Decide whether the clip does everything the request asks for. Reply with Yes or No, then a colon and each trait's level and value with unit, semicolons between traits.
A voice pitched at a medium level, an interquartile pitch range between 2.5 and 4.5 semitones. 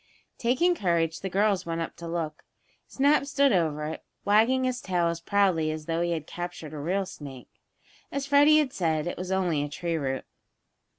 No: medium, 175 Hz; average, 5.0 semitones